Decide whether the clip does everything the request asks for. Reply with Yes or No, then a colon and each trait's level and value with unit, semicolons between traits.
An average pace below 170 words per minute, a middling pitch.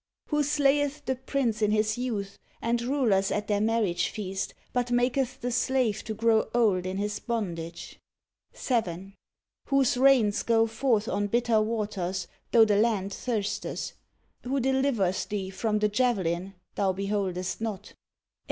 No: average, 145 wpm; high, 220 Hz